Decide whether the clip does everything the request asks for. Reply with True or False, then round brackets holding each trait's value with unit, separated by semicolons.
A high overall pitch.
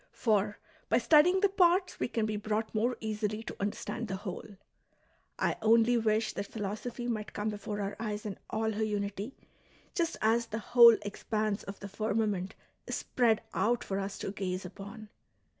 True (215 Hz)